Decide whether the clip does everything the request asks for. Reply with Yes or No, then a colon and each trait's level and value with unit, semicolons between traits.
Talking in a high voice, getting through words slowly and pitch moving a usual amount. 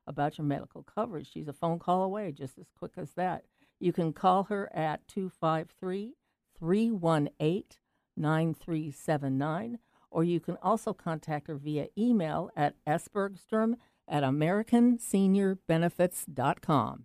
No: medium, 170 Hz; slow, 115 wpm; average, 4.3 semitones